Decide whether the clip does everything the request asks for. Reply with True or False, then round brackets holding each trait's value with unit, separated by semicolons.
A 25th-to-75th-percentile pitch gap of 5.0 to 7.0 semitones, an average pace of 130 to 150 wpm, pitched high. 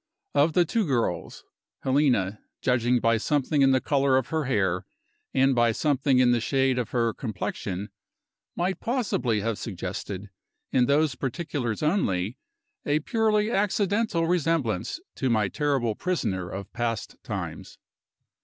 False (5.4 semitones; 135 wpm; 130 Hz)